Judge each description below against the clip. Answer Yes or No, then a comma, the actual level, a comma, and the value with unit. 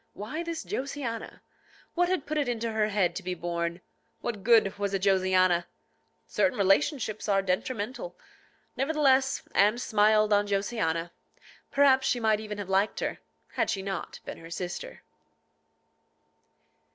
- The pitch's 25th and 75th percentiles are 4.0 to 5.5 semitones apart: Yes, average, 5.2 semitones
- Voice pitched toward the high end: Yes, high, 210 Hz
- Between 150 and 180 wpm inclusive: No, average, 140 wpm